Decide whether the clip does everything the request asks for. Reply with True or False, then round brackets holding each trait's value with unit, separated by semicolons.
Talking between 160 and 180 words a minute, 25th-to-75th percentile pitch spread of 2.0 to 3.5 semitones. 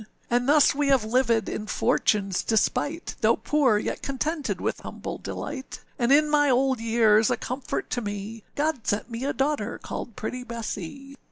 False (170 wpm; 4.0 semitones)